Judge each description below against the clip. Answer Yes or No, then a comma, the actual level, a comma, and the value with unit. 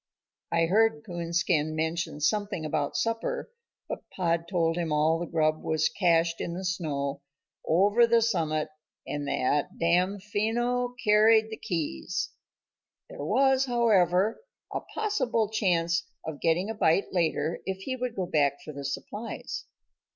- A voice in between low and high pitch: Yes, medium, 175 Hz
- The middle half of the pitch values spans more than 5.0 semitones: Yes, wide, 5.4 semitones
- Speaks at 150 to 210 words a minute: No, average, 140 wpm